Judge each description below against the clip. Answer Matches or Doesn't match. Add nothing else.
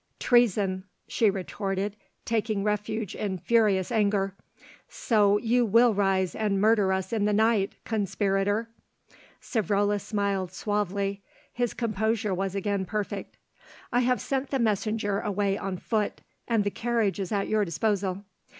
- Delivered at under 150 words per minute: Matches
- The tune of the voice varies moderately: Doesn't match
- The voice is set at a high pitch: Matches